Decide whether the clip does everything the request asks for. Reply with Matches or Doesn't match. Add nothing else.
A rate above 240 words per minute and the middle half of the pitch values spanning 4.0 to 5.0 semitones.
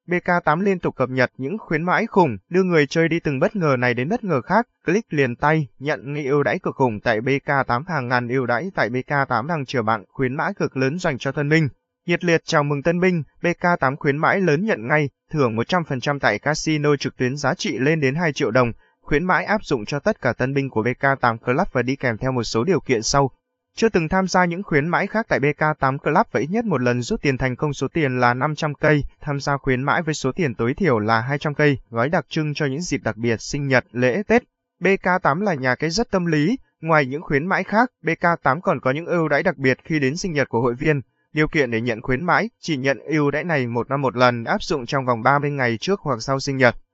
Matches